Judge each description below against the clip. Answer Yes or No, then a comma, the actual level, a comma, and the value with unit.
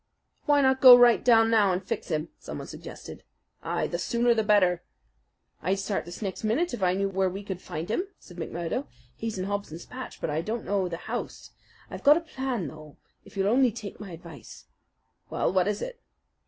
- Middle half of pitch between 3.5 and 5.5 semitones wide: Yes, average, 5.0 semitones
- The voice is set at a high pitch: Yes, high, 200 Hz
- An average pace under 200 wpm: No, fast, 205 wpm